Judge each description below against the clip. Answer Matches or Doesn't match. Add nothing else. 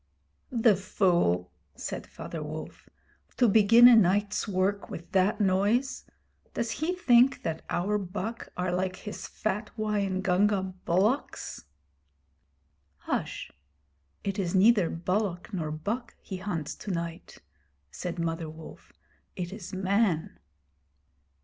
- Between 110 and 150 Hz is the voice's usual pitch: Doesn't match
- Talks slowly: Matches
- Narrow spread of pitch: Doesn't match